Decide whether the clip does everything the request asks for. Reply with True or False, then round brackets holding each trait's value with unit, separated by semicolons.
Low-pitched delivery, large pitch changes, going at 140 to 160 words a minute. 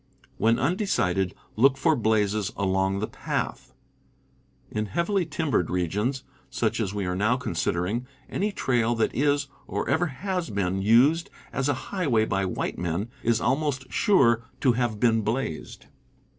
True (115 Hz; 6.1 semitones; 150 wpm)